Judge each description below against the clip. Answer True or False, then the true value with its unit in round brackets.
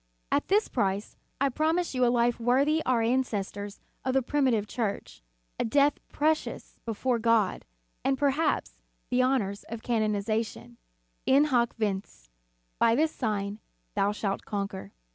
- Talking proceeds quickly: False (140 wpm)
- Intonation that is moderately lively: True (4.6 semitones)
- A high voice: True (235 Hz)